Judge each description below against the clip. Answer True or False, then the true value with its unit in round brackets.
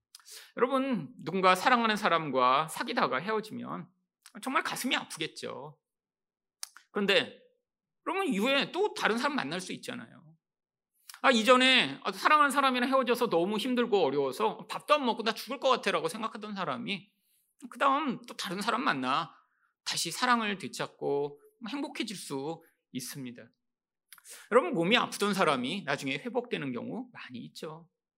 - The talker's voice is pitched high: True (220 Hz)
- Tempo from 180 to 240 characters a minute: False (315 characters per minute)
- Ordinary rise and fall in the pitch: False (6.9 semitones)